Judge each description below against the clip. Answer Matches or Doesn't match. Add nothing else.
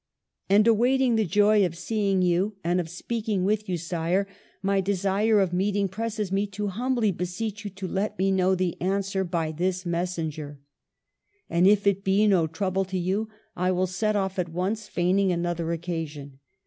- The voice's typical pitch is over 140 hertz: Matches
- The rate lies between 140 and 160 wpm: Doesn't match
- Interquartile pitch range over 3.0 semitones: Doesn't match